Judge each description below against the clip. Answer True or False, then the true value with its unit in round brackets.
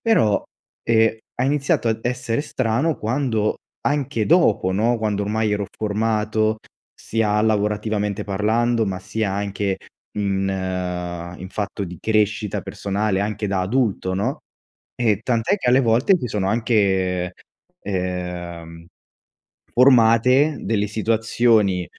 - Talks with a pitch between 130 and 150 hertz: False (105 Hz)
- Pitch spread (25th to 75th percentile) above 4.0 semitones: False (2.9 semitones)